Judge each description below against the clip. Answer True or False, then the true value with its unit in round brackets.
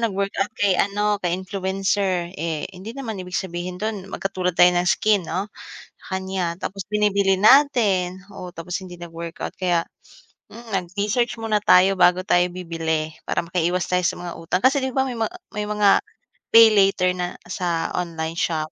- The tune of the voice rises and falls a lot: False (2.6 semitones)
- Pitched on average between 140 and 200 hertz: True (185 Hz)